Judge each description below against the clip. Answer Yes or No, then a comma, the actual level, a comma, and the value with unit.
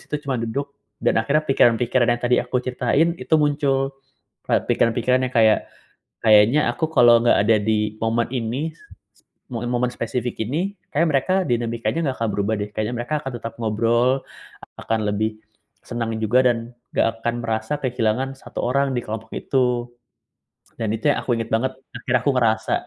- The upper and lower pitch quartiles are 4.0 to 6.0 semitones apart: No, average, 2.9 semitones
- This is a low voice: Yes, low, 120 Hz